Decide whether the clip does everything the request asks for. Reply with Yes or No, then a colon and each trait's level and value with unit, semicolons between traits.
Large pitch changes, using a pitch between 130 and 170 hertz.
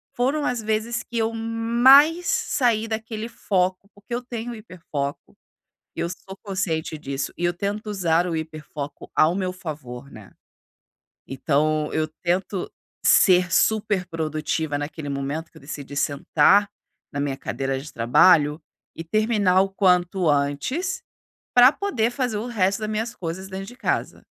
No: wide, 6.2 semitones; medium, 185 Hz